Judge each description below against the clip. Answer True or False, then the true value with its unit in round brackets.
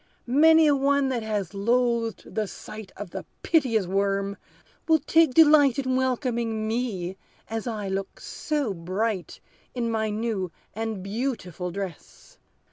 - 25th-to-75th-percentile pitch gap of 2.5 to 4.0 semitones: False (4.7 semitones)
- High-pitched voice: True (225 Hz)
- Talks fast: False (135 wpm)